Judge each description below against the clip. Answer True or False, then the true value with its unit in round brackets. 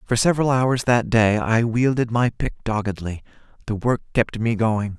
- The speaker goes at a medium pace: True (180 wpm)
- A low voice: True (115 Hz)